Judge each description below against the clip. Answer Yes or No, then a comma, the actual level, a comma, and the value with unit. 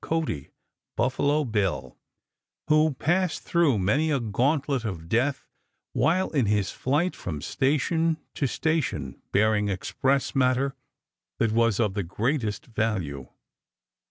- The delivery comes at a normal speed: No, slow, 120 wpm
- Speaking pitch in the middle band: No, low, 125 Hz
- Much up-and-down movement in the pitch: Yes, wide, 6.4 semitones